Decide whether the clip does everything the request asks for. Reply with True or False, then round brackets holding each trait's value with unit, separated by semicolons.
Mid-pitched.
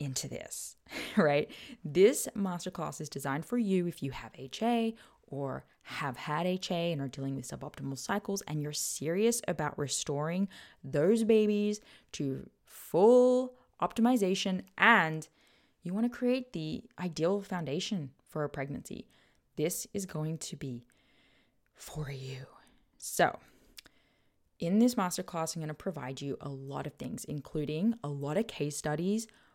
True (170 Hz)